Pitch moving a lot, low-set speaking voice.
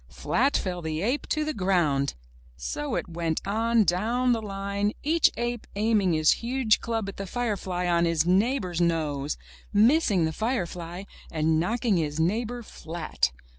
No: wide, 5.7 semitones; high, 195 Hz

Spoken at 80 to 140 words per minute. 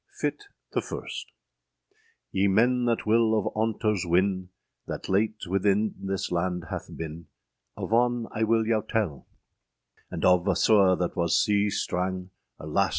No: average, 155 wpm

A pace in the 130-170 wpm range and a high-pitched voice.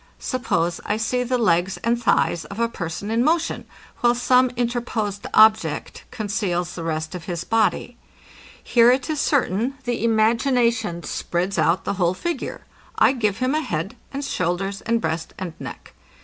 Yes: average, 165 wpm; high, 220 Hz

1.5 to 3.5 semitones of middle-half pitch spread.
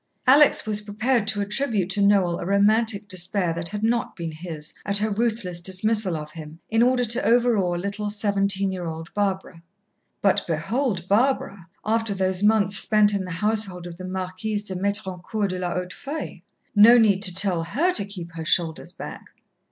Yes: average, 3.2 semitones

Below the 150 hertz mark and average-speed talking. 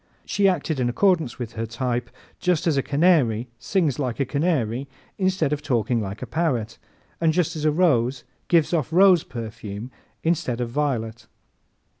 Yes: medium, 140 Hz; average, 165 wpm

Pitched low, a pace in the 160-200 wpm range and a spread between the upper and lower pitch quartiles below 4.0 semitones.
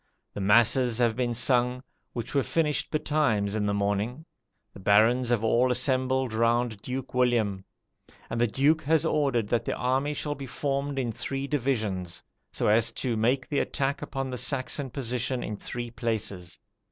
Yes: low, 125 Hz; average, 165 wpm; average, 3.4 semitones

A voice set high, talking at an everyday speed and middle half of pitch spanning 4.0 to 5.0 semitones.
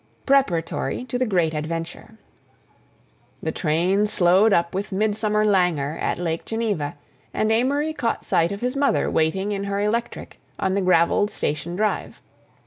Yes: high, 200 Hz; average, 145 wpm; average, 4.5 semitones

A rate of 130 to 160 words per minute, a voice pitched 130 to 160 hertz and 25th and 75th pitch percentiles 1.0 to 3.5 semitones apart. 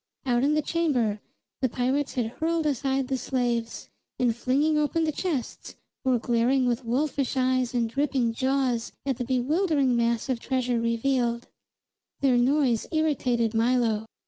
No: average, 145 wpm; very high, 255 Hz; average, 2.9 semitones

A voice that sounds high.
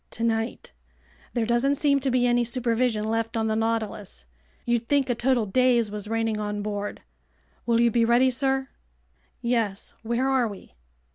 Yes: high, 235 Hz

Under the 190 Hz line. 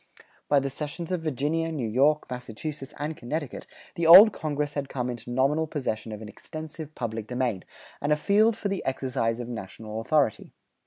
Yes: medium, 140 Hz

